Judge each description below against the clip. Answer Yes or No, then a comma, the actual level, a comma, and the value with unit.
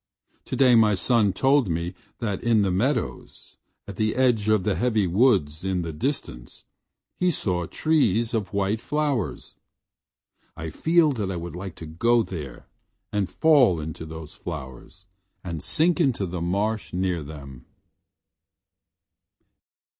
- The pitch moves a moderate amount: No, wide, 5.9 semitones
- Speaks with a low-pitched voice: Yes, low, 100 Hz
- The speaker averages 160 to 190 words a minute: No, average, 140 wpm